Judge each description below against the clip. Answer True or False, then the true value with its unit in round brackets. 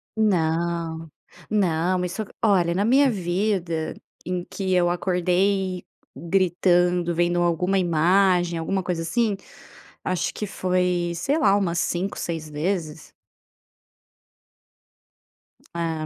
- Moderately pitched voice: True (180 Hz)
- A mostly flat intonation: True (2.1 semitones)